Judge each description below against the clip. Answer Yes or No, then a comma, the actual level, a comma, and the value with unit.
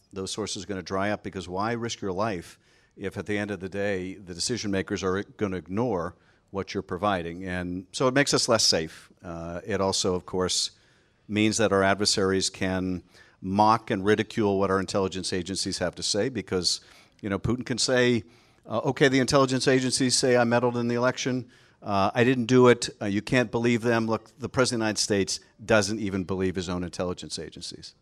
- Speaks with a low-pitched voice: Yes, low, 100 Hz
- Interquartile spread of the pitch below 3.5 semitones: No, average, 3.9 semitones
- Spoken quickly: Yes, fast, 210 wpm